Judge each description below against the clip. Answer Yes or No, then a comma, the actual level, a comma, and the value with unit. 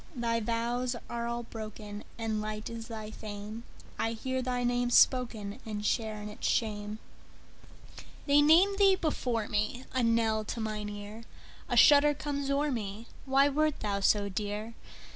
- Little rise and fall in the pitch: No, average, 3.2 semitones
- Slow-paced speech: Yes, slow, 130 wpm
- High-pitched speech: Yes, high, 230 Hz